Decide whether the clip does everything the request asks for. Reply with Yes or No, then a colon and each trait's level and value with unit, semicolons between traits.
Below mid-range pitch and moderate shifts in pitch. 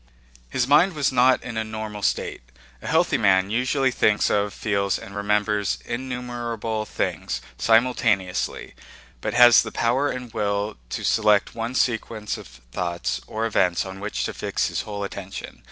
Yes: low, 110 Hz; average, 3.3 semitones